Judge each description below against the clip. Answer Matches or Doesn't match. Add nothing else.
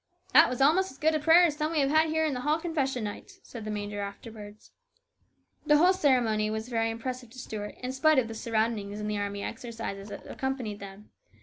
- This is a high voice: Matches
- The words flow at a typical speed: Doesn't match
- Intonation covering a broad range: Matches